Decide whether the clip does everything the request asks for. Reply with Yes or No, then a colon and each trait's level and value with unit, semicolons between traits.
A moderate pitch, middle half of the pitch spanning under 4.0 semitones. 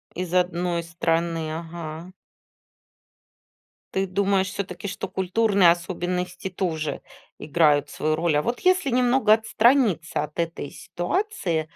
Yes: medium, 180 Hz; average, 3.3 semitones